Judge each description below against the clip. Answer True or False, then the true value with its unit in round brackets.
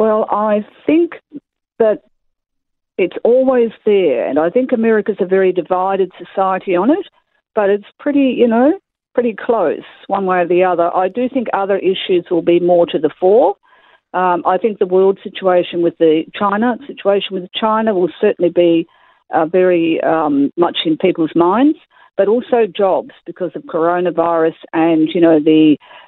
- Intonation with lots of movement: True (5.8 semitones)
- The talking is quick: False (170 wpm)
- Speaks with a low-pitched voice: False (195 Hz)